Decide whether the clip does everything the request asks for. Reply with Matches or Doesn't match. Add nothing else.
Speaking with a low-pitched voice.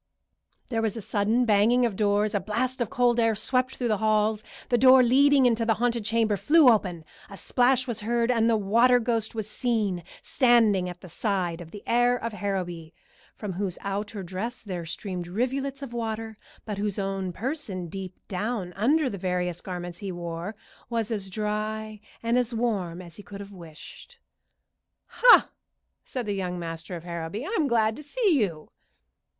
Doesn't match